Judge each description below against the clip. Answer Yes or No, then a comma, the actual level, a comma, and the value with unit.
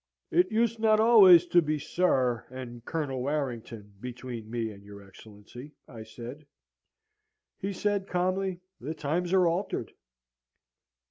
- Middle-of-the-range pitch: Yes, medium, 145 Hz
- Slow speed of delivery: Yes, slow, 130 wpm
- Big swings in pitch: Yes, wide, 7.4 semitones